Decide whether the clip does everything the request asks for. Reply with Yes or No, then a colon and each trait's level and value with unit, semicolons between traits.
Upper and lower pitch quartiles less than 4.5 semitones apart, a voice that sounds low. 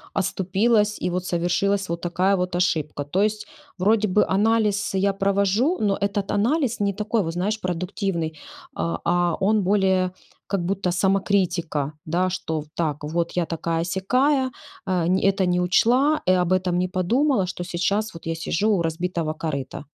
No: average, 2.9 semitones; medium, 185 Hz